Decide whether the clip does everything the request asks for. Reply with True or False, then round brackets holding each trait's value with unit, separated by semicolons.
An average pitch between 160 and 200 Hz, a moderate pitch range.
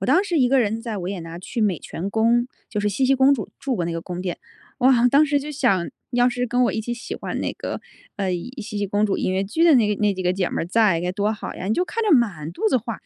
False (220 Hz; 4.7 semitones)